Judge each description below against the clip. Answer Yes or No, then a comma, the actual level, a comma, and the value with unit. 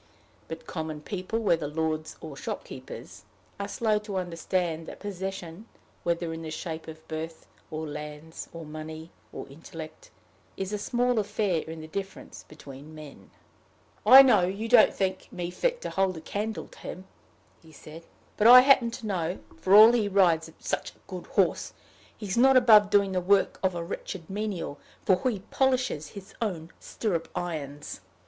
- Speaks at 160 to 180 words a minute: Yes, average, 170 wpm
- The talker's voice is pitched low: No, medium, 180 Hz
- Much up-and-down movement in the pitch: No, average, 4.6 semitones